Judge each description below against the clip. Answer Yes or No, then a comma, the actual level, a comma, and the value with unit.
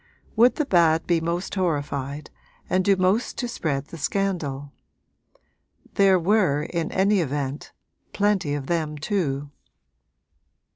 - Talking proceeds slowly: Yes, slow, 125 wpm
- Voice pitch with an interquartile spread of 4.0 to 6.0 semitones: Yes, average, 5.1 semitones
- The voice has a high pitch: No, medium, 170 Hz